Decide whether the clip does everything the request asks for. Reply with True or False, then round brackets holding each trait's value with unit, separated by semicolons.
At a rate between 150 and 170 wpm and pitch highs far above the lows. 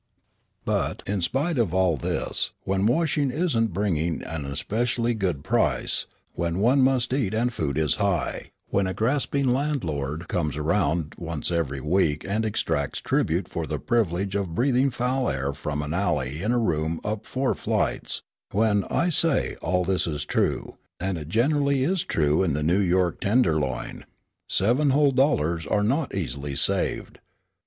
True (160 wpm; 7.5 semitones)